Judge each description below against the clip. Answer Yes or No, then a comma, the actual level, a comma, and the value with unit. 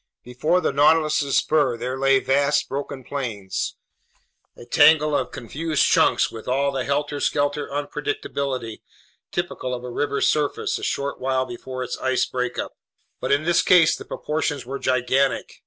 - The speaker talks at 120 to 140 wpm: No, average, 155 wpm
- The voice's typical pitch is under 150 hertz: Yes, medium, 140 Hz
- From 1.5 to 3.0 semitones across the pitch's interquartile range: Yes, narrow, 2.6 semitones